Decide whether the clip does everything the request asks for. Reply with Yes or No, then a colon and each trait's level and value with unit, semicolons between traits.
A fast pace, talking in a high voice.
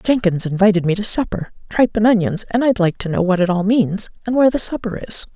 Yes: fast, 245 wpm; high, 205 Hz